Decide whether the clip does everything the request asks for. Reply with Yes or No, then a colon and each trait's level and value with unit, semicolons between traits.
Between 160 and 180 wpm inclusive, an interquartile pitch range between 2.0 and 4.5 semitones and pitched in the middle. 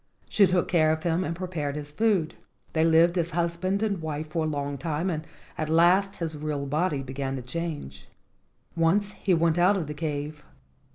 No: average, 190 wpm; average, 2.8 semitones; medium, 160 Hz